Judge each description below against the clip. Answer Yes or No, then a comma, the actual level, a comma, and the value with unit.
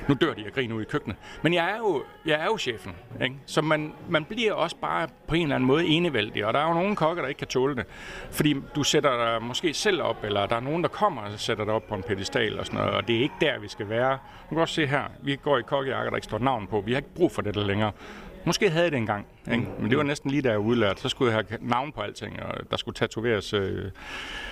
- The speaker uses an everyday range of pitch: No, wide, 6.1 semitones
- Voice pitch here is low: Yes, low, 130 Hz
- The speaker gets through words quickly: Yes, fast, 290 wpm